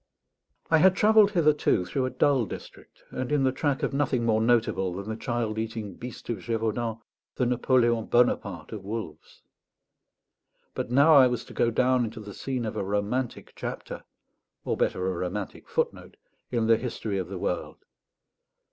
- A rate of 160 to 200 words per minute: Yes, average, 170 wpm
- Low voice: Yes, low, 115 Hz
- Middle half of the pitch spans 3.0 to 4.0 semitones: Yes, average, 3.6 semitones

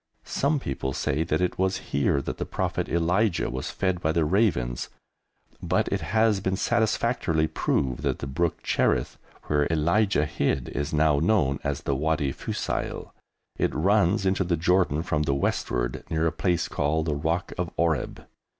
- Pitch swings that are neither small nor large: Yes, average, 4.5 semitones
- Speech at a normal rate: Yes, average, 170 wpm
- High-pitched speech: No, very low, 80 Hz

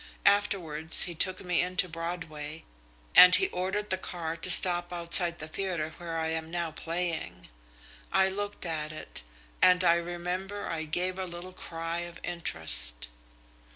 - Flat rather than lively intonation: Yes, narrow, 2.1 semitones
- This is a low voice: No, medium, 175 Hz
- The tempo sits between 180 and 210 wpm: No, average, 155 wpm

